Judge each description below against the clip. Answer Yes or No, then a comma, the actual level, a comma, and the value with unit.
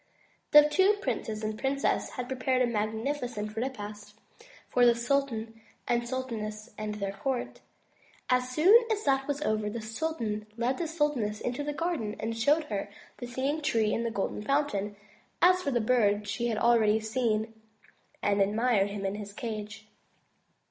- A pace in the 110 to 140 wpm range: No, average, 165 wpm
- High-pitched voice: Yes, high, 235 Hz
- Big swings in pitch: No, average, 4.2 semitones